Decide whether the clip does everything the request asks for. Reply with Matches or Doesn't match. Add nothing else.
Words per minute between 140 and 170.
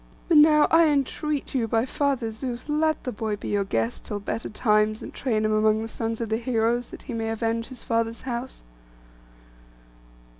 Doesn't match